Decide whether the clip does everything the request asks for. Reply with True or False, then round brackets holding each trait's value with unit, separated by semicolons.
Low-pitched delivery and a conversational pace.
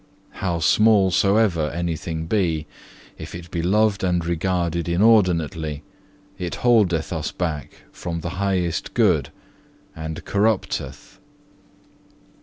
False (85 Hz; 105 wpm)